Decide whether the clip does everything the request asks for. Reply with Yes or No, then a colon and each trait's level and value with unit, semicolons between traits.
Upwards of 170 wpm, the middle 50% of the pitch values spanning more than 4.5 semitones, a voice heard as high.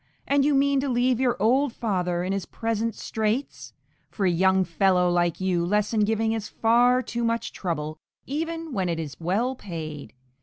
Yes: average, 180 wpm; wide, 5.5 semitones; high, 215 Hz